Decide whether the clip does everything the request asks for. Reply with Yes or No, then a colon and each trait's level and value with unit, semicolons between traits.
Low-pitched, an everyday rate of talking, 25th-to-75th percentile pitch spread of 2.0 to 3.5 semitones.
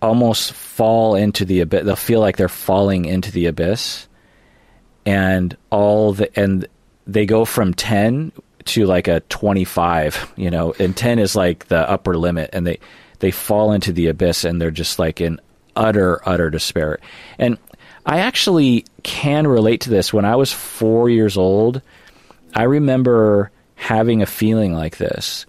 No: low, 100 Hz; average, 165 wpm; average, 4.1 semitones